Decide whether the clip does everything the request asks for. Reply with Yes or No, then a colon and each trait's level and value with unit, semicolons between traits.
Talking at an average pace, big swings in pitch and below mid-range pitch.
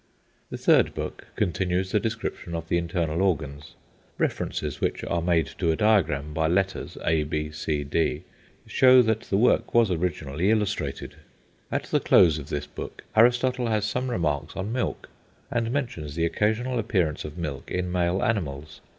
Yes: average, 165 wpm; wide, 6.1 semitones; very low, 90 Hz